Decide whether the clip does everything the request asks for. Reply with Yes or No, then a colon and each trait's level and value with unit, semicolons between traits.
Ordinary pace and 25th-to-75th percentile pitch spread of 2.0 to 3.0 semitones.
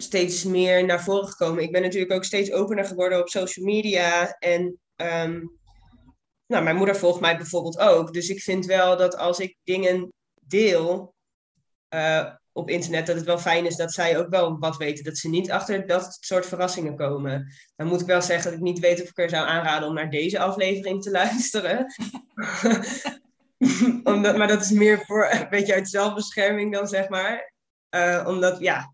Yes: average, 190 wpm; average, 2.7 semitones